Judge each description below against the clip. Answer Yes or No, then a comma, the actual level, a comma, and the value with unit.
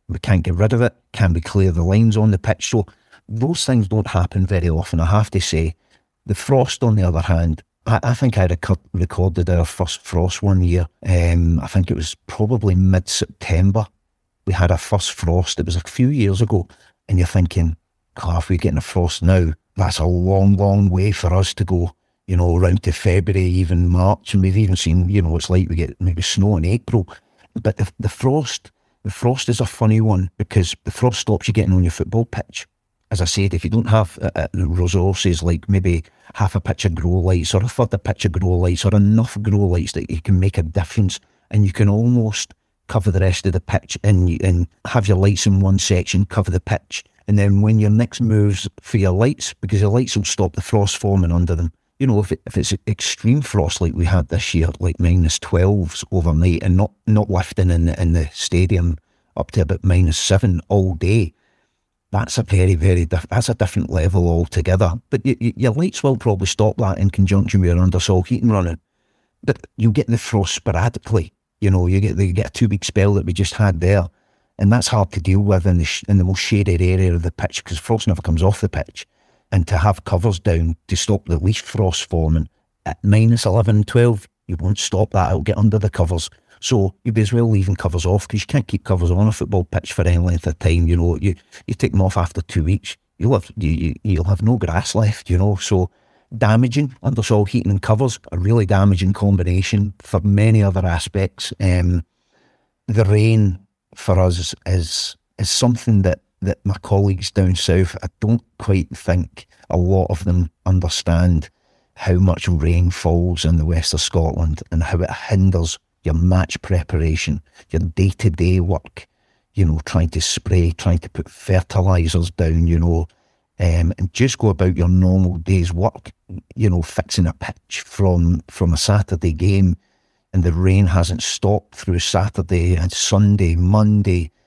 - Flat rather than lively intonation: No, average, 3.0 semitones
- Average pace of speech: No, fast, 210 wpm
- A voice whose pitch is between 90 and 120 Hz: Yes, very low, 95 Hz